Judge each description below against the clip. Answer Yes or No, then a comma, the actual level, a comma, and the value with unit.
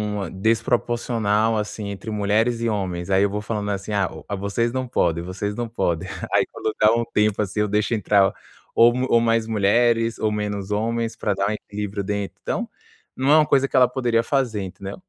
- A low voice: Yes, low, 105 Hz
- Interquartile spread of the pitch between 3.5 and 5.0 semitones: No, narrow, 2.5 semitones